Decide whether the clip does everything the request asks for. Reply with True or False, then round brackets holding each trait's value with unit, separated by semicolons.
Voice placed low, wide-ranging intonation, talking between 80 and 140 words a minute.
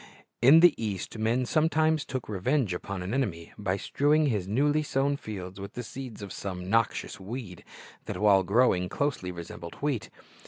False (110 Hz; 6.5 semitones; 165 wpm)